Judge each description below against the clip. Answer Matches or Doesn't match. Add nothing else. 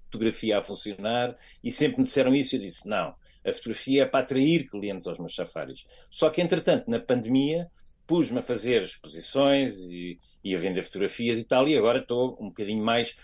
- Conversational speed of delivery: Doesn't match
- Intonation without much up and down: Doesn't match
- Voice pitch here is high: Doesn't match